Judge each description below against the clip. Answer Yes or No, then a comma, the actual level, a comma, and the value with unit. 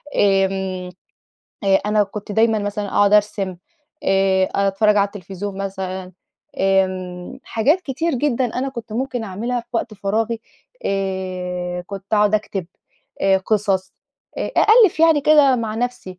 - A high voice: Yes, high, 205 Hz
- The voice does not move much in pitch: No, average, 3.2 semitones